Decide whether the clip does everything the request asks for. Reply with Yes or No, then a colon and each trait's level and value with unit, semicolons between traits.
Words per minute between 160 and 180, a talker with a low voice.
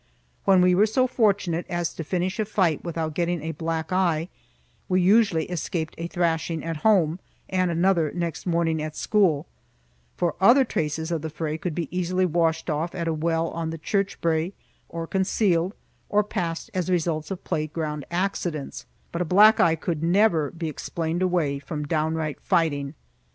No: average, 170 wpm; medium, 170 Hz